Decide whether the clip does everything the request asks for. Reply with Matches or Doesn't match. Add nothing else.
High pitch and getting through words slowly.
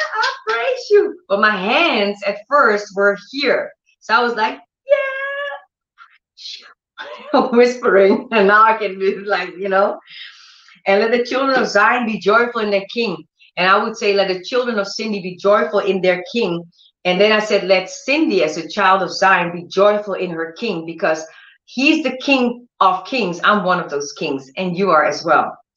Doesn't match